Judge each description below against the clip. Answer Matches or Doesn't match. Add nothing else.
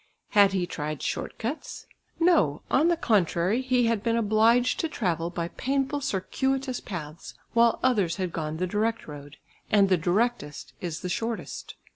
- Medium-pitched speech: Doesn't match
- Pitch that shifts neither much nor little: Doesn't match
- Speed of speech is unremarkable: Matches